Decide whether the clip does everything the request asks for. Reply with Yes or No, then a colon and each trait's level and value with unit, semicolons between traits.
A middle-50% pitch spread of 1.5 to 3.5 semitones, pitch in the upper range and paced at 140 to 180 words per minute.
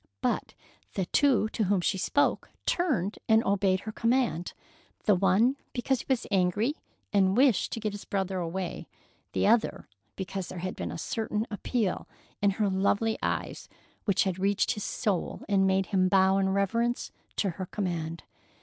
Yes: average, 2.9 semitones; high, 200 Hz; average, 170 wpm